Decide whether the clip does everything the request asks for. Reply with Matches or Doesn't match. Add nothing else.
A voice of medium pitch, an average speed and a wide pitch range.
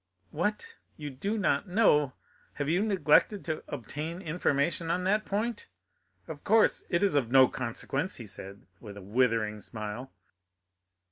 Matches